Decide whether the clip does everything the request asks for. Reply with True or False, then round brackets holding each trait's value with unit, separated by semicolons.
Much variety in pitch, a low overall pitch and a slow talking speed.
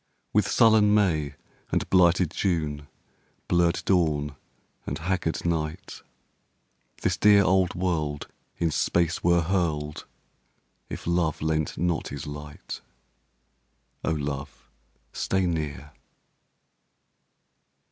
False (3.5 semitones; 85 Hz; 95 wpm)